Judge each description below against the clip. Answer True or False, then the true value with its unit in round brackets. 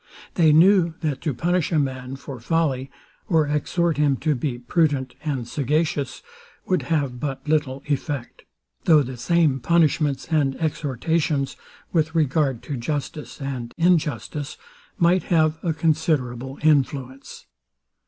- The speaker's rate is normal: False (130 wpm)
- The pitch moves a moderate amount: True (3.2 semitones)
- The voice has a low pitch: False (150 Hz)